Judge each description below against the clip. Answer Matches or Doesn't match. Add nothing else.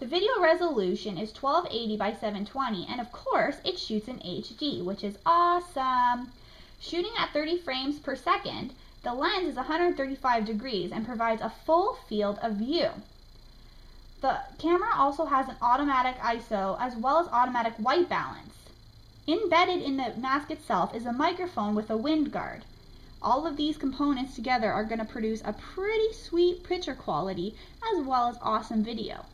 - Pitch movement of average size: Doesn't match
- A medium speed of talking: Matches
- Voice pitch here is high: Matches